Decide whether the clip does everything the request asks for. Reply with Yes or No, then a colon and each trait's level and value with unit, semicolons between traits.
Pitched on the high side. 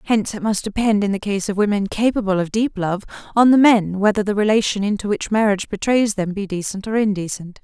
Yes: high, 205 Hz